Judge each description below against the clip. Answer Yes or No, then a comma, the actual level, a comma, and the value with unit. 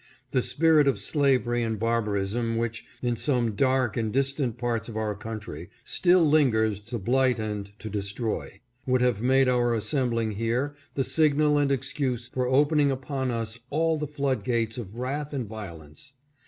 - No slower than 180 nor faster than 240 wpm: No, average, 170 wpm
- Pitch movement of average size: Yes, average, 3.7 semitones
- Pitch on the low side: Yes, low, 120 Hz